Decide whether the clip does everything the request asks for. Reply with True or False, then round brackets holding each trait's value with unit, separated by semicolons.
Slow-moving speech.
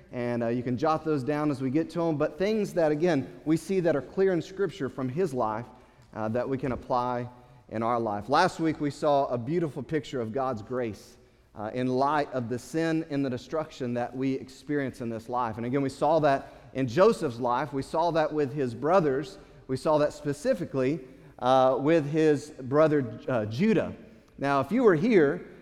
False (205 wpm)